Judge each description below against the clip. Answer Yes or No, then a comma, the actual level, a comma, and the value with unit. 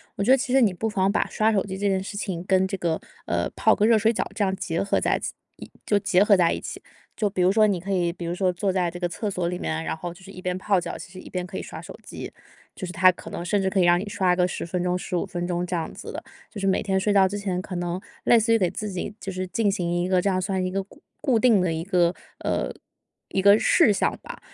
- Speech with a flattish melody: Yes, narrow, 2.1 semitones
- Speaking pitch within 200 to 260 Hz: No, high, 190 Hz